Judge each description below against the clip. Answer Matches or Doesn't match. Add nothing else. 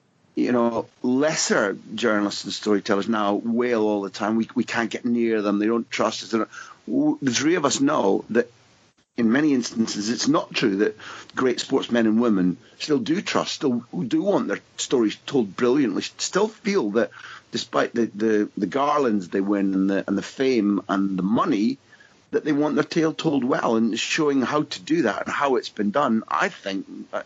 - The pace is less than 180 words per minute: Doesn't match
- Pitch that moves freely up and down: Matches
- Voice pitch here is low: Matches